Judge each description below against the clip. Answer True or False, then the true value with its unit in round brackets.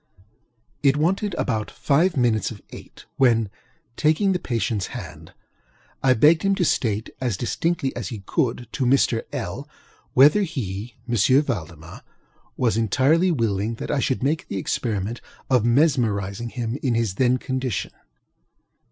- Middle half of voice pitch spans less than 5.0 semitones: True (4.6 semitones)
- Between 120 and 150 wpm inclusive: True (145 wpm)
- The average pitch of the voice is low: True (125 Hz)